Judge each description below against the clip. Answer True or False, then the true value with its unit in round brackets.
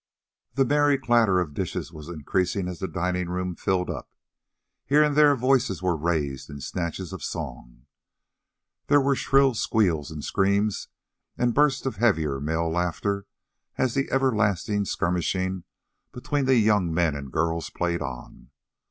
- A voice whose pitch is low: True (95 Hz)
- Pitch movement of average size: False (6.7 semitones)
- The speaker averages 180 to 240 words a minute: False (150 wpm)